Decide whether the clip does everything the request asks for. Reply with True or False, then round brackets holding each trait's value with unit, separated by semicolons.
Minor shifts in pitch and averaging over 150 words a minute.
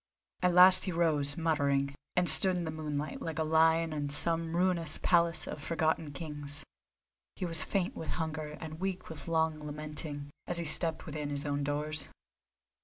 True (2.1 semitones; 175 wpm)